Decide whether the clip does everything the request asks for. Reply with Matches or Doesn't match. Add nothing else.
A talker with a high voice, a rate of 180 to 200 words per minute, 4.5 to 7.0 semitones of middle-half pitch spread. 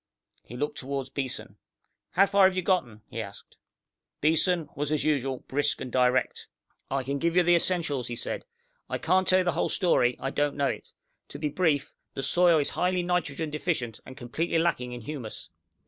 Doesn't match